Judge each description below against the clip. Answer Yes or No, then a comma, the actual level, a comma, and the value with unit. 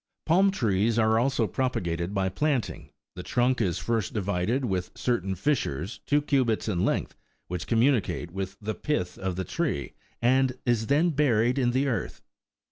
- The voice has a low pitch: Yes, low, 115 Hz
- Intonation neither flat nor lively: No, wide, 5.7 semitones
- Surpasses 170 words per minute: No, average, 165 wpm